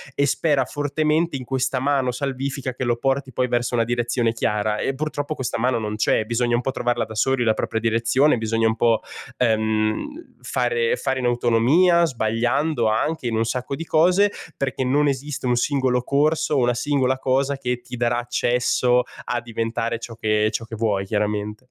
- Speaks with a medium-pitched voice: No, low, 125 Hz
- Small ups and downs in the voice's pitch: No, average, 3.3 semitones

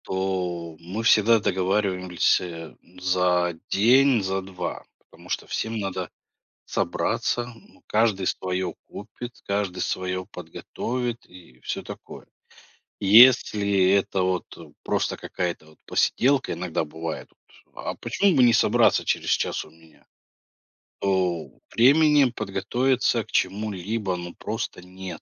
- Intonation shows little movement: No, average, 3.8 semitones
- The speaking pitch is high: No, very low, 95 Hz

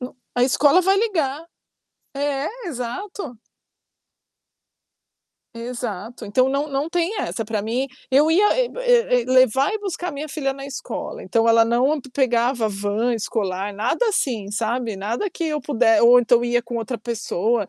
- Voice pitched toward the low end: No, very high, 250 Hz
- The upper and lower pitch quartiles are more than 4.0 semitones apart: Yes, average, 4.4 semitones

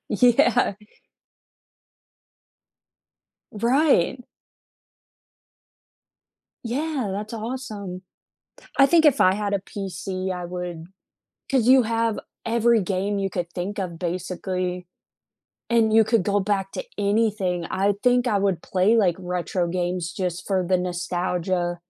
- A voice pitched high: Yes, high, 195 Hz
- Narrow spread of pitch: No, average, 4.1 semitones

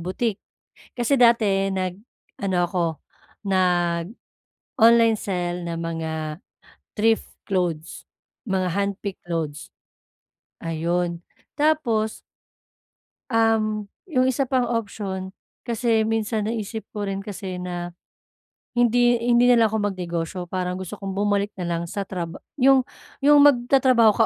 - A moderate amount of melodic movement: Yes, average, 4.3 semitones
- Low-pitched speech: No, high, 200 Hz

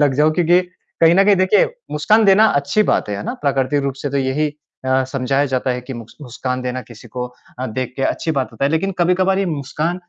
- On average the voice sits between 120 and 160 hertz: Yes, medium, 140 Hz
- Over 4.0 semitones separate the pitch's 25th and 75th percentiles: Yes, average, 5.2 semitones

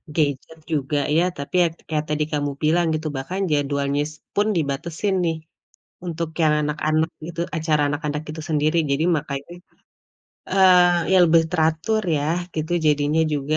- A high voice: No, medium, 155 Hz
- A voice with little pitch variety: Yes, narrow, 2.3 semitones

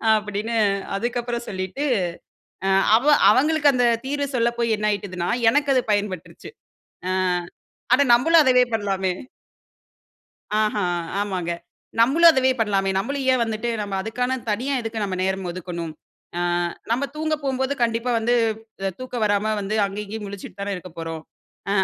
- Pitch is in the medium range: No, high, 220 Hz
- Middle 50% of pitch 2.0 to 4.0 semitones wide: No, average, 4.5 semitones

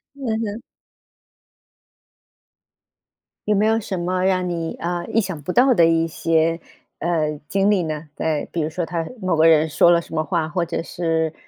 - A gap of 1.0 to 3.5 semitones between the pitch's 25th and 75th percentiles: Yes, narrow, 2.6 semitones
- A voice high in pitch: No, medium, 170 Hz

